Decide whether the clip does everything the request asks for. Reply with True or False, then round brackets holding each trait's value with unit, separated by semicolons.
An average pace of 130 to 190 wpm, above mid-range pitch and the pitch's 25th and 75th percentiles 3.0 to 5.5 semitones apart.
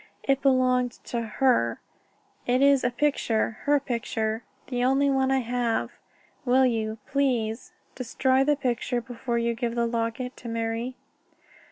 False (150 wpm; 245 Hz; 2.4 semitones)